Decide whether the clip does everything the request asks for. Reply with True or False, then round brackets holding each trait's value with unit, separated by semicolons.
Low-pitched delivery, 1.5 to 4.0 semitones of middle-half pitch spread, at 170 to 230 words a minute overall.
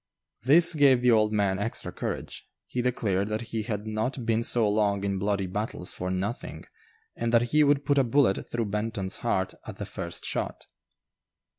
True (110 Hz; 3.4 semitones; 180 wpm)